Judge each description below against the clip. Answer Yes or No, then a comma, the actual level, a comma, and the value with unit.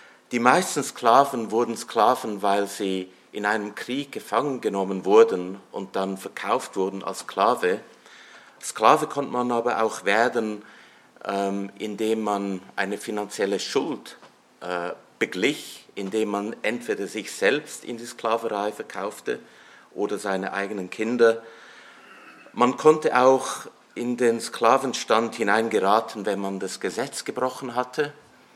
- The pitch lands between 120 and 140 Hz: No, low, 110 Hz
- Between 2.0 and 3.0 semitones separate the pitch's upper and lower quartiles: No, average, 3.7 semitones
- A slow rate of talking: Yes, slow, 120 wpm